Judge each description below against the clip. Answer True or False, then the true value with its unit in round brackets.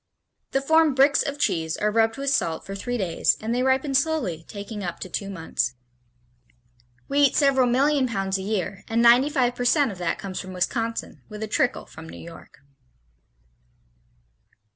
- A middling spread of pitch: False (6.0 semitones)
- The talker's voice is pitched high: True (230 Hz)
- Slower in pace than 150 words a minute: False (170 wpm)